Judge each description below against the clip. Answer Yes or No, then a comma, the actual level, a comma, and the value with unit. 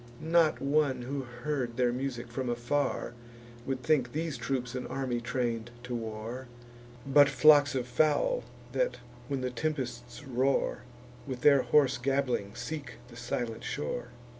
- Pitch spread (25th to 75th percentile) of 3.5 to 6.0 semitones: No, average, 2.9 semitones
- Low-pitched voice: Yes, low, 130 Hz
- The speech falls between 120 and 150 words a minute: Yes, average, 140 wpm